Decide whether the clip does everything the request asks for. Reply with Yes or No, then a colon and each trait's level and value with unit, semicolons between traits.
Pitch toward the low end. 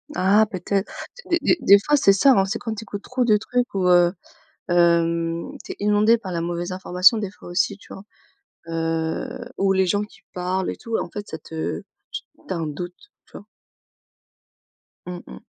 No: high, 190 Hz